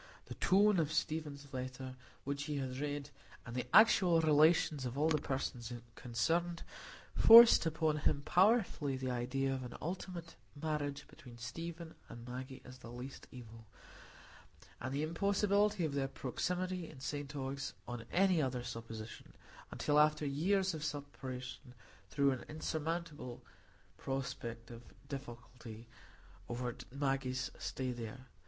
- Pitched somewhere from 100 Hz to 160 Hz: Yes, medium, 140 Hz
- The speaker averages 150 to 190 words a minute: No, slow, 135 wpm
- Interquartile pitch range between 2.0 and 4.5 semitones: Yes, average, 4.1 semitones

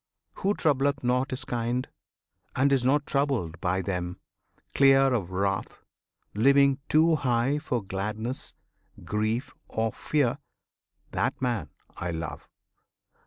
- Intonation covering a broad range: Yes, wide, 5.9 semitones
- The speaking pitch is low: Yes, low, 125 Hz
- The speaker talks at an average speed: No, slow, 120 wpm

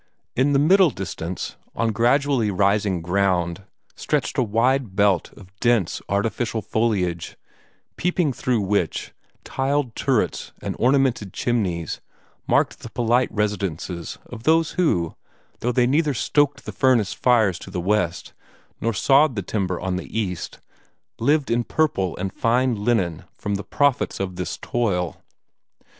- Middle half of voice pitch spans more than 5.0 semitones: Yes, wide, 5.4 semitones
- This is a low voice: Yes, low, 110 Hz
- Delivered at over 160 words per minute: No, average, 140 wpm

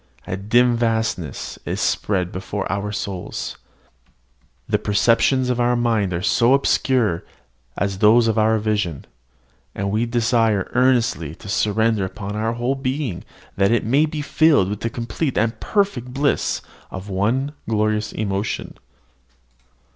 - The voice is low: Yes, low, 110 Hz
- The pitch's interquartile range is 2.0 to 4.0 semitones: Yes, average, 3.5 semitones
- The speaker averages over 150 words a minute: No, average, 140 wpm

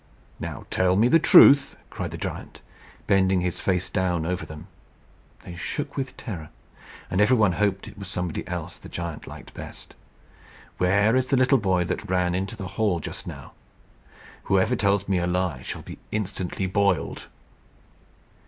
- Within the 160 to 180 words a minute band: Yes, average, 165 wpm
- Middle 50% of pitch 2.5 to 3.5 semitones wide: Yes, average, 2.9 semitones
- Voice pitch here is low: Yes, very low, 95 Hz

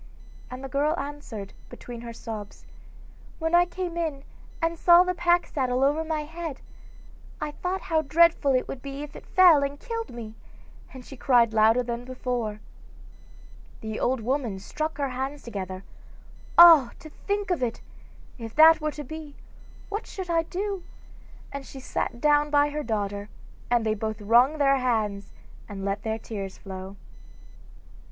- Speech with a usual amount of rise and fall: No, wide, 5.8 semitones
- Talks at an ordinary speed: Yes, average, 165 wpm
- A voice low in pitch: No, very high, 275 Hz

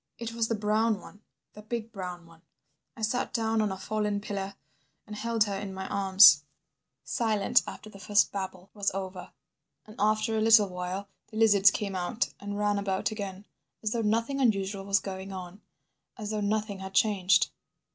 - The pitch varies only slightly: Yes, narrow, 2.1 semitones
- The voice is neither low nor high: No, high, 205 Hz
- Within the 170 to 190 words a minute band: Yes, average, 180 wpm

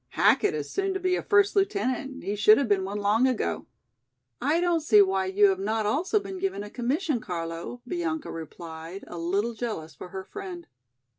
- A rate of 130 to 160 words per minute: No, average, 195 wpm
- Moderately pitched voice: No, high, 225 Hz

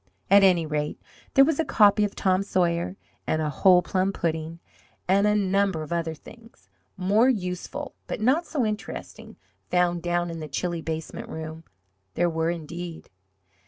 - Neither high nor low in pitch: Yes, medium, 180 Hz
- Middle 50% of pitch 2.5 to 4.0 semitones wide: Yes, average, 3.7 semitones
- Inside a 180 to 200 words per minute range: No, average, 160 wpm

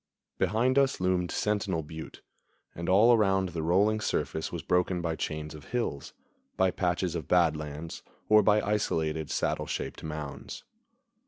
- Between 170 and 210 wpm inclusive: No, average, 150 wpm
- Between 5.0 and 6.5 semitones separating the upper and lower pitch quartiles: No, average, 4.5 semitones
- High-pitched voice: No, very low, 90 Hz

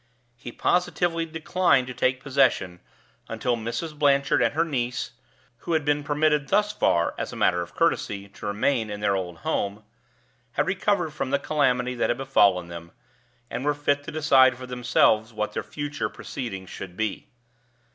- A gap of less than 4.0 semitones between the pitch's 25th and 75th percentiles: No, wide, 5.5 semitones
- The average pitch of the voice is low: Yes, low, 130 Hz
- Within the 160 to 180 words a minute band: Yes, average, 170 wpm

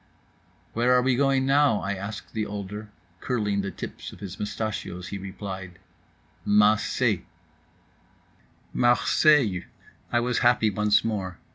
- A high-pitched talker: No, low, 105 Hz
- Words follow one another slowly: Yes, slow, 130 wpm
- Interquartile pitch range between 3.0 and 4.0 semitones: Yes, average, 3.4 semitones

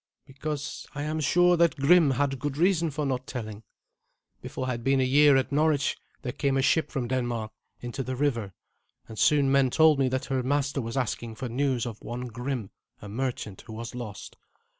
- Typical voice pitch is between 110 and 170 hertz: Yes, low, 135 Hz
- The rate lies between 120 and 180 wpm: No, average, 200 wpm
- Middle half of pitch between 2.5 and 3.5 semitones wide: Yes, average, 3.1 semitones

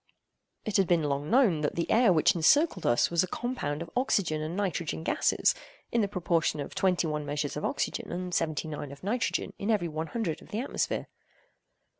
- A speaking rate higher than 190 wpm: Yes, average, 200 wpm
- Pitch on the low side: No, medium, 170 Hz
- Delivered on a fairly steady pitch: No, average, 4.8 semitones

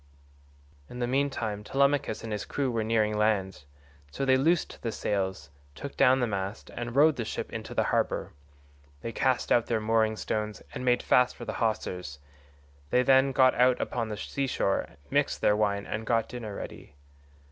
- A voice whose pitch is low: Yes, low, 115 Hz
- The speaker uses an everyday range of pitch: Yes, average, 3.7 semitones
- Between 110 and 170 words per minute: No, average, 180 wpm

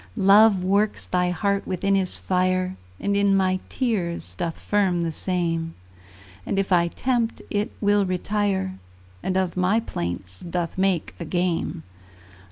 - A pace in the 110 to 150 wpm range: Yes, average, 145 wpm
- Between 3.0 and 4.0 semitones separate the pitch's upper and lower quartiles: No, narrow, 2.5 semitones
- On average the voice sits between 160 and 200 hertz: Yes, medium, 185 Hz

